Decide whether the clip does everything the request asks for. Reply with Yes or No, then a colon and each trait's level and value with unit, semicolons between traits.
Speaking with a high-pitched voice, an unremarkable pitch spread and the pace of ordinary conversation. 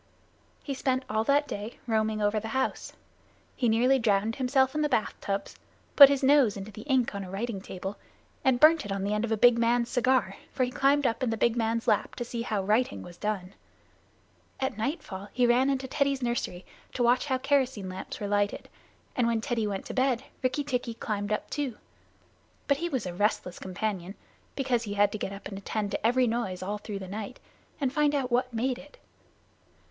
No: high, 235 Hz; average, 4.2 semitones; fast, 210 wpm